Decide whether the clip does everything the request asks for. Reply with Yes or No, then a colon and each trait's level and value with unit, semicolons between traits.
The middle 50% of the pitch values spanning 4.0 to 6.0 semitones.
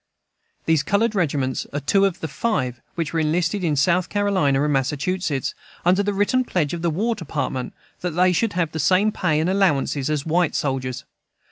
Yes: average, 4.8 semitones